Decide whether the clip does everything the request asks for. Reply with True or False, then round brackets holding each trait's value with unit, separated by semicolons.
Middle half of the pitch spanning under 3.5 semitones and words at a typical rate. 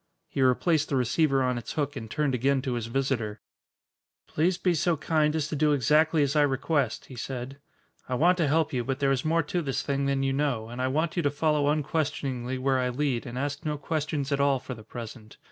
False (3.0 semitones; 230 wpm)